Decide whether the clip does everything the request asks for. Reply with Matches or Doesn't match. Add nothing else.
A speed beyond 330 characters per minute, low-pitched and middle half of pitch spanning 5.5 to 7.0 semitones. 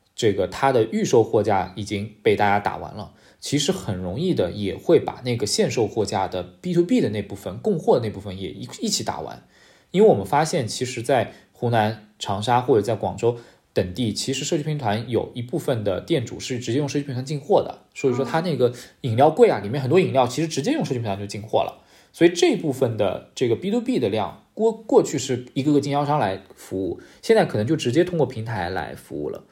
Matches